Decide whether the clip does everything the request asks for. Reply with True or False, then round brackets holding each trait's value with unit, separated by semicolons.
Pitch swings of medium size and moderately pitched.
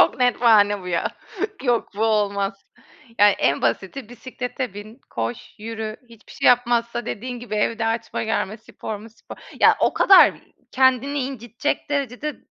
False (3.2 semitones; 230 Hz)